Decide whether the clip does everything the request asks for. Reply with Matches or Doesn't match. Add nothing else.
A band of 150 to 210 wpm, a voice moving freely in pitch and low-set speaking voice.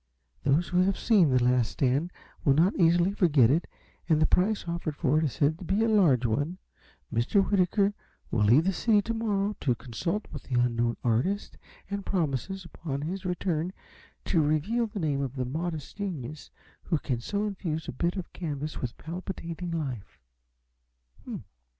Doesn't match